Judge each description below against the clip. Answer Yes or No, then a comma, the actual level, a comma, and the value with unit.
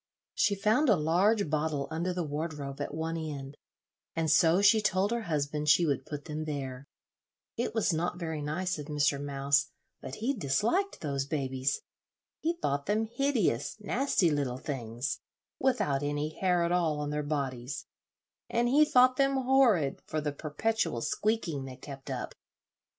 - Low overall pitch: No, medium, 155 Hz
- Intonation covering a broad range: Yes, wide, 6.5 semitones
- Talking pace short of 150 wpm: No, average, 160 wpm